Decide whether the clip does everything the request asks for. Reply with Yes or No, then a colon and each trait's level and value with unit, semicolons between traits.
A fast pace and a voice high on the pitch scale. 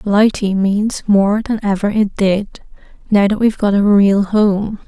No: average, 170 wpm; high, 205 Hz